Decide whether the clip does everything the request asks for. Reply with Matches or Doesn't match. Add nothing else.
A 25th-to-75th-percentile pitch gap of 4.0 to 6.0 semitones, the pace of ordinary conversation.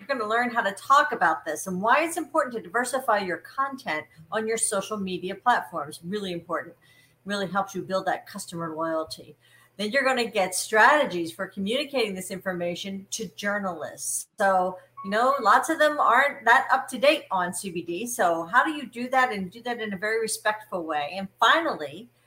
Matches